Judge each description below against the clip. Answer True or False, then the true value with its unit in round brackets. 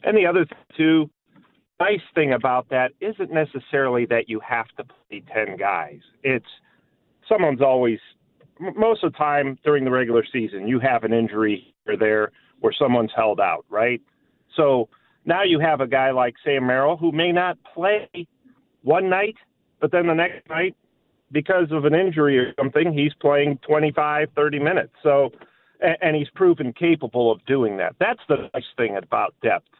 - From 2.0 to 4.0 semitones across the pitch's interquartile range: False (4.6 semitones)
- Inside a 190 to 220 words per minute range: False (170 wpm)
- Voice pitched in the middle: True (145 Hz)